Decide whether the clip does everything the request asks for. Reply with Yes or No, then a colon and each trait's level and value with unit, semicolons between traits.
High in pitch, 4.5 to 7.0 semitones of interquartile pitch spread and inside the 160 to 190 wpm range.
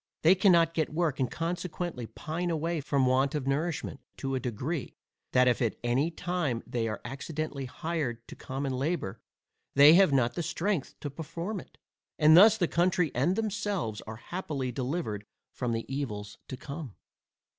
No: medium, 145 Hz; average, 5.1 semitones; average, 165 wpm